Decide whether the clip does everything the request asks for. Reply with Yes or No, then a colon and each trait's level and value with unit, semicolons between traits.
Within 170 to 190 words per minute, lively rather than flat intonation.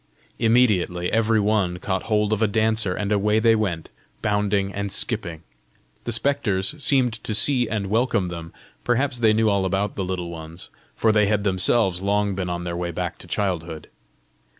No: average, 175 wpm; average, 3.2 semitones